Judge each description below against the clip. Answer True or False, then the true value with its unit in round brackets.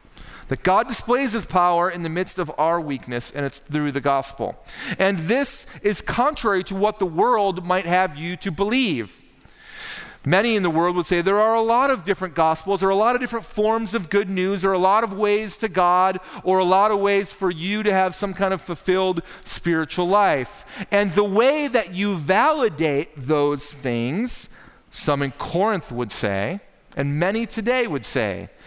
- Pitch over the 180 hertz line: True (190 Hz)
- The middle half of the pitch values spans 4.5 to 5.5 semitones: False (3.8 semitones)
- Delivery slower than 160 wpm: False (195 wpm)